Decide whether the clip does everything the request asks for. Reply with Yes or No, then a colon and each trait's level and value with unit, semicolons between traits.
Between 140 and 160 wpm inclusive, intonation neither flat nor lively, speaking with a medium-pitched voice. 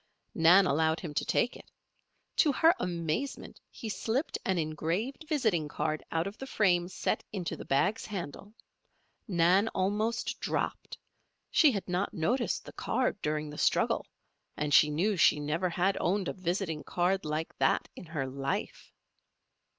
Yes: average, 155 wpm; average, 4.8 semitones; medium, 180 Hz